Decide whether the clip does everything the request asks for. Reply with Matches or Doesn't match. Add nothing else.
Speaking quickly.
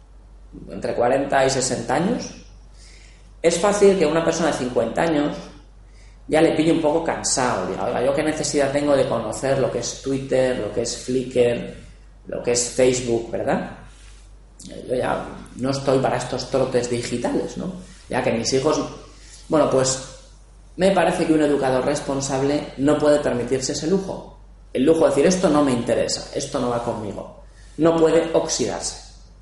Doesn't match